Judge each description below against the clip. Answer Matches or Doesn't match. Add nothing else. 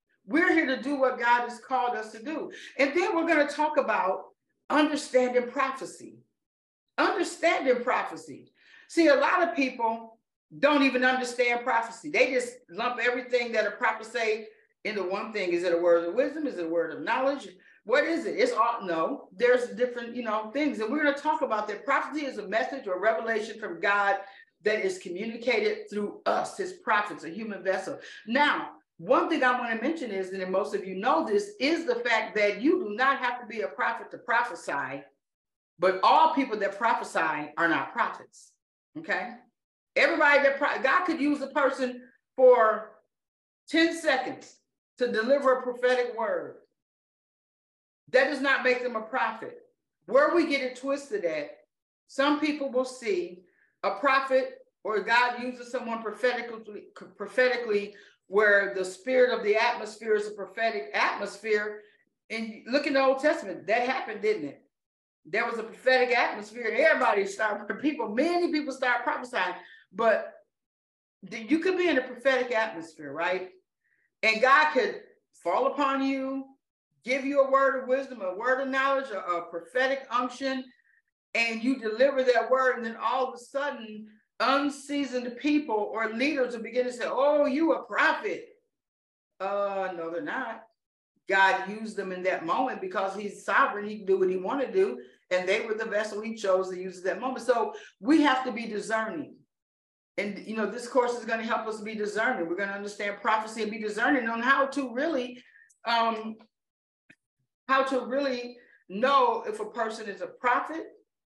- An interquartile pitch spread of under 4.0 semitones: Doesn't match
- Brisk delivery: Doesn't match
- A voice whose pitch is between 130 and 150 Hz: Doesn't match